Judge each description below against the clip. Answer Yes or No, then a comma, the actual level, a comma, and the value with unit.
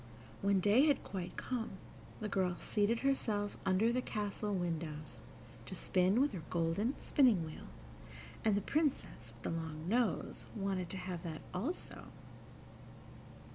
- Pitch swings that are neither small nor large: Yes, average, 4.7 semitones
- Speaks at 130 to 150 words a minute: Yes, average, 140 wpm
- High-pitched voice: Yes, high, 195 Hz